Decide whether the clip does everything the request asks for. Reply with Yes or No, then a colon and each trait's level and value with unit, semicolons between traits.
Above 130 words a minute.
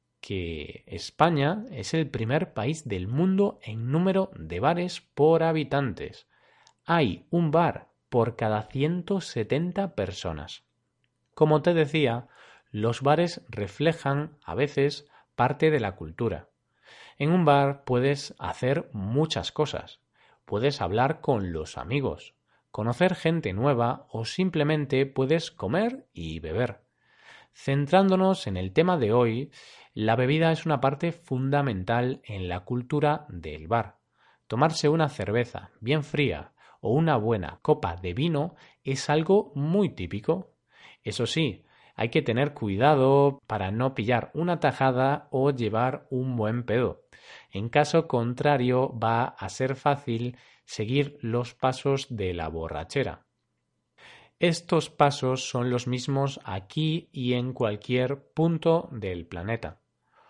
No: slow, 125 wpm